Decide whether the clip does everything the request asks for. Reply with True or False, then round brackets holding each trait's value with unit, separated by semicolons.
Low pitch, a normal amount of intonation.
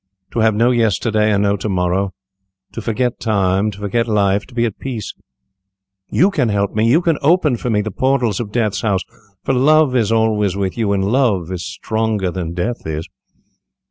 True (110 Hz; 3.3 semitones)